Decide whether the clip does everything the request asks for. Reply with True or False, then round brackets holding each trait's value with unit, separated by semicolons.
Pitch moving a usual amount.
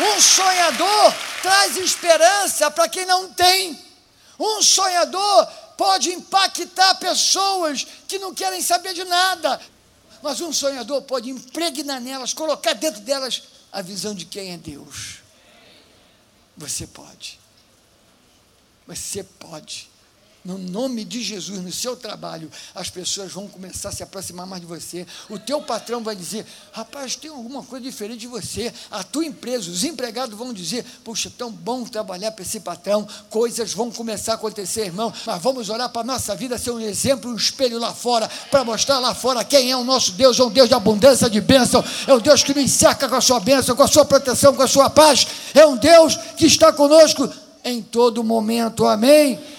False (5.7 semitones)